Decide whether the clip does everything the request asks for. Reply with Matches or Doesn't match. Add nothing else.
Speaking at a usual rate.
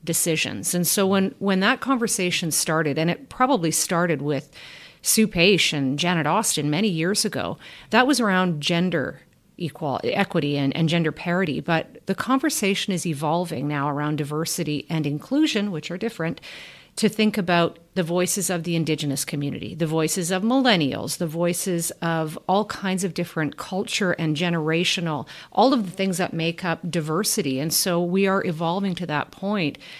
Matches